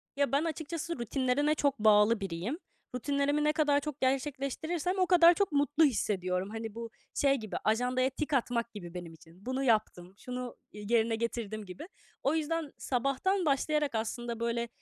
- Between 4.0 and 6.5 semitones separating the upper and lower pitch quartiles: Yes, average, 5.0 semitones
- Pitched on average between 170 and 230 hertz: No, very high, 255 Hz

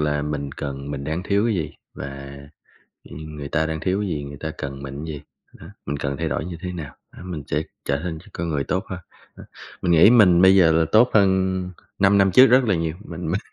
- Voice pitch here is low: Yes, very low, 80 Hz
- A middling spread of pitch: Yes, average, 4.5 semitones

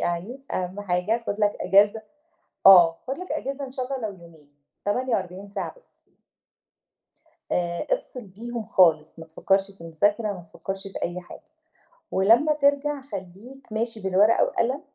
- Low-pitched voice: No, high, 205 Hz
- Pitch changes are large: Yes, wide, 5.7 semitones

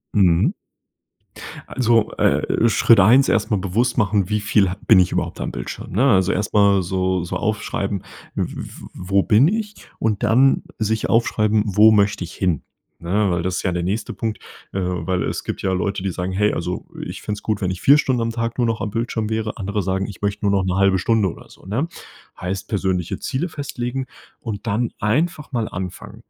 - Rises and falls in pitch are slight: No, average, 3.3 semitones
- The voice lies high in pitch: No, low, 105 Hz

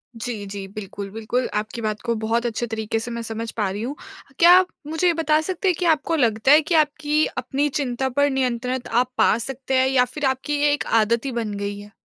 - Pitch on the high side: Yes, very high, 250 Hz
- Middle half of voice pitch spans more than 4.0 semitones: Yes, average, 4.7 semitones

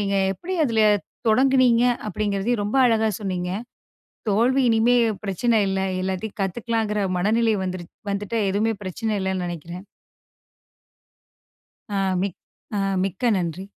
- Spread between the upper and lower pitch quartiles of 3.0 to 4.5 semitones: Yes, average, 3.4 semitones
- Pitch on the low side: No, high, 205 Hz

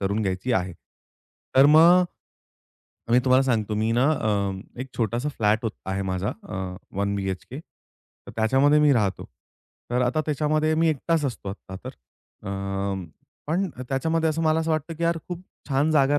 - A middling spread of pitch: No, wide, 6.8 semitones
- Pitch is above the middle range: No, low, 135 Hz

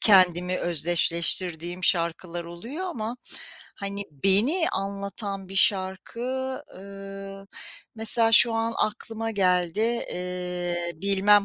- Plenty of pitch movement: No, average, 3.3 semitones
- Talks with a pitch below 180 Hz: No, high, 195 Hz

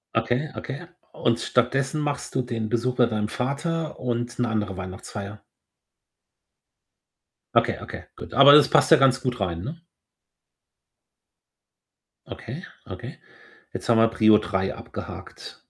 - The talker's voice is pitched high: No, low, 120 Hz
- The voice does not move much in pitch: No, average, 3.9 semitones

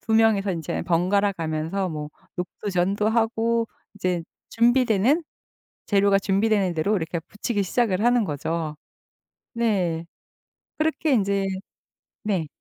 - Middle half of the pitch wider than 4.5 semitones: No, average, 4.1 semitones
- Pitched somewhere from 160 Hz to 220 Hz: Yes, high, 200 Hz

